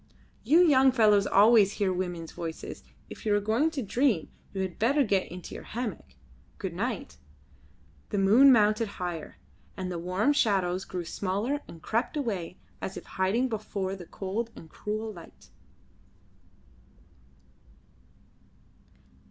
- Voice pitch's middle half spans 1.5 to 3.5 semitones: No, average, 4.1 semitones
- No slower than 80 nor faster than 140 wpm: Yes, slow, 135 wpm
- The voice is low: No, high, 205 Hz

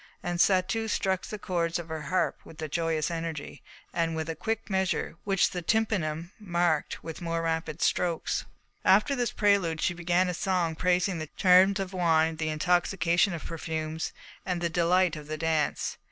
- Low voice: No, medium, 170 Hz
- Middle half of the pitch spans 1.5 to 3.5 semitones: Yes, narrow, 2.5 semitones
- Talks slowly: No, average, 170 wpm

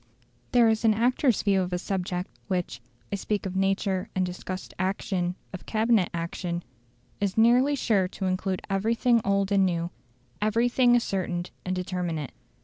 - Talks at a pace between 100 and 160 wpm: Yes, average, 150 wpm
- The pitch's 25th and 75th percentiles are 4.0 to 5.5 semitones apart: No, average, 3.3 semitones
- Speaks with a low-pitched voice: No, high, 195 Hz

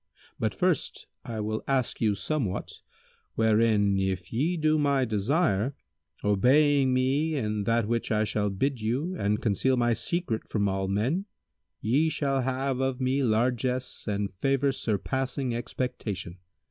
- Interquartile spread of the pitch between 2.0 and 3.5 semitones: No, average, 4.4 semitones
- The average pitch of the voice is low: Yes, low, 120 Hz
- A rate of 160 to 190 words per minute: No, average, 140 wpm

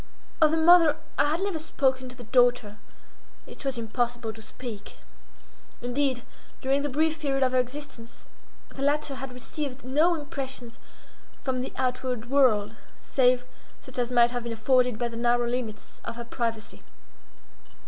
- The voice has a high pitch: Yes, very high, 255 Hz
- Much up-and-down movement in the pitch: No, average, 2.8 semitones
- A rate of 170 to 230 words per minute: No, average, 155 wpm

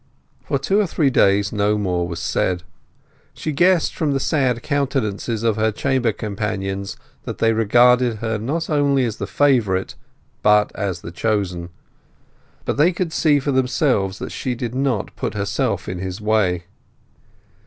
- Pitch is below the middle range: Yes, low, 110 Hz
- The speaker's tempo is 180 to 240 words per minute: No, average, 160 wpm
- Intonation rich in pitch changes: Yes, wide, 5.7 semitones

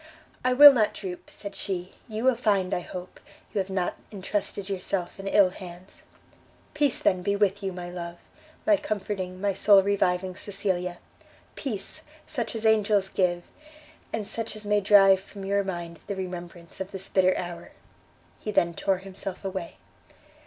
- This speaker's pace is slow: No, average, 165 wpm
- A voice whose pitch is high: Yes, high, 195 Hz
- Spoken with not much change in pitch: Yes, narrow, 2.2 semitones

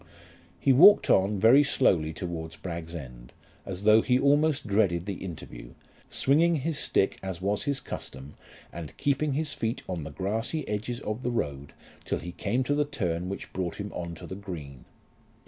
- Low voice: Yes, low, 100 Hz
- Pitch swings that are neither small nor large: No, wide, 7.6 semitones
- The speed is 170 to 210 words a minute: Yes, average, 180 wpm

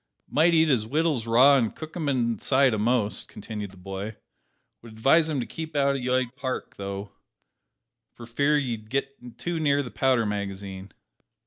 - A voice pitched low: Yes, low, 125 Hz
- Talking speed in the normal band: Yes, average, 165 wpm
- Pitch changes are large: No, average, 4.8 semitones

